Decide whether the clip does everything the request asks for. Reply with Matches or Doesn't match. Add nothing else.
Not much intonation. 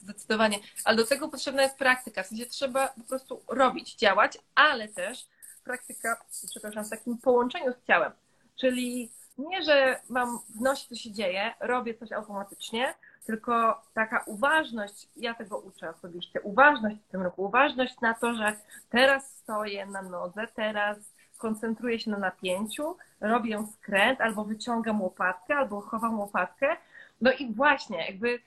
Doesn't match